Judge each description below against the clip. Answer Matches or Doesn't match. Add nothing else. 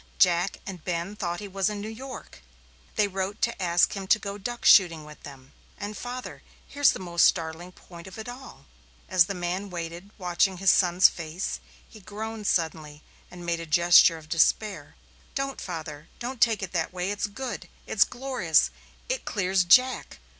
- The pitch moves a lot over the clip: Doesn't match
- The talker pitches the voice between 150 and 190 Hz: Matches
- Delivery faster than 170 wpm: Matches